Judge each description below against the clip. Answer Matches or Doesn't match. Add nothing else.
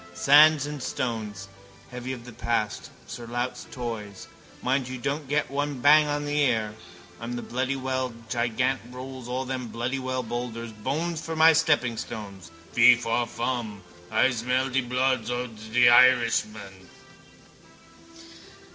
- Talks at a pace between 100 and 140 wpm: Matches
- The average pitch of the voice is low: Matches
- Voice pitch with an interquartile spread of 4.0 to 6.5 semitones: Doesn't match